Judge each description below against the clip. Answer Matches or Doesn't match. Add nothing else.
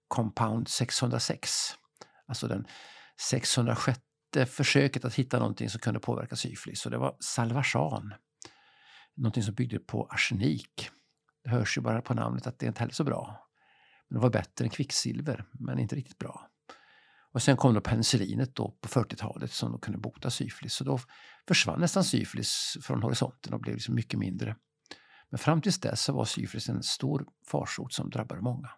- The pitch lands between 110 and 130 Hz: Matches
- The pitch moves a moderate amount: Matches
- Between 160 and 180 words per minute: Matches